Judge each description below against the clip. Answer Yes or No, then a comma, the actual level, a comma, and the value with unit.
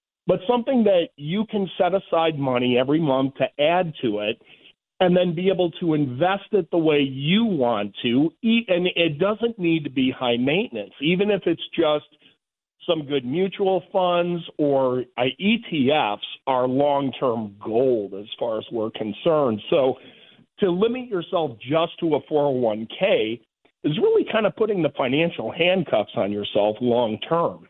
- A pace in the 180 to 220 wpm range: No, average, 160 wpm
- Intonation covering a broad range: Yes, wide, 6.3 semitones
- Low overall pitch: No, medium, 165 Hz